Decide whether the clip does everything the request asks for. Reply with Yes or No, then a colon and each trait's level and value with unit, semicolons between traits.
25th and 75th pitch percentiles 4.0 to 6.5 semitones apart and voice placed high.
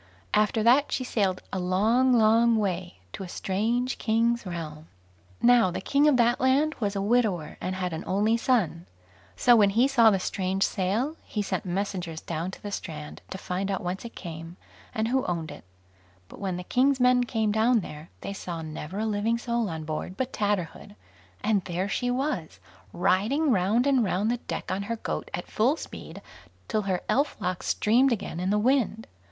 Yes: average, 4.6 semitones; high, 210 Hz